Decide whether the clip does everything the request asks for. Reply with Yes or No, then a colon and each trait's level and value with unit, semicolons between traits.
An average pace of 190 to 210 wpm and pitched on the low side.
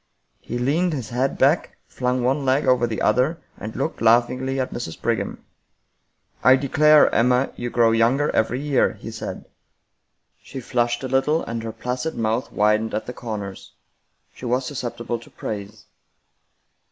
No: average, 160 wpm; low, 125 Hz